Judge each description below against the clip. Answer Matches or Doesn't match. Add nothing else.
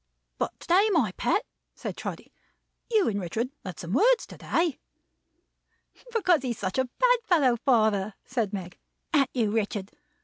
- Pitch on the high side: Matches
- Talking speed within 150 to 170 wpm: Matches